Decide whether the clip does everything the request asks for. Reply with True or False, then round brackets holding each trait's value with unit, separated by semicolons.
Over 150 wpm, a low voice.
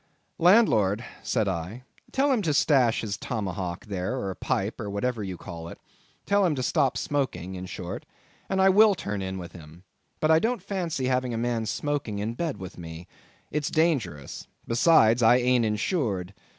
True (175 wpm; 115 Hz)